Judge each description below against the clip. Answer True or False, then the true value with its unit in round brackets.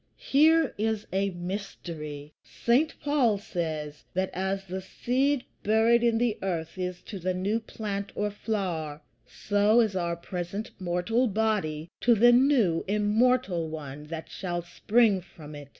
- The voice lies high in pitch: True (195 Hz)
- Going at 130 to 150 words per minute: True (145 wpm)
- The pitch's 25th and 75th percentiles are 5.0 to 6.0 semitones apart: False (4.6 semitones)